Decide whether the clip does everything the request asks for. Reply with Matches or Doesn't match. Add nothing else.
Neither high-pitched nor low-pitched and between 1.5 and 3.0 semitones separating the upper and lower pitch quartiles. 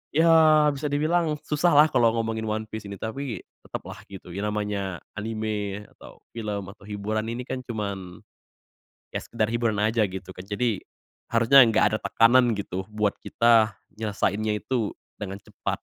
Doesn't match